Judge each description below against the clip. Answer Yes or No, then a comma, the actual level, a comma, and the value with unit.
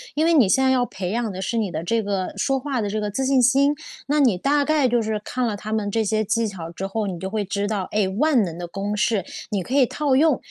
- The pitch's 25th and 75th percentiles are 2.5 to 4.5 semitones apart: No, average, 4.9 semitones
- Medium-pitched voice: No, high, 220 Hz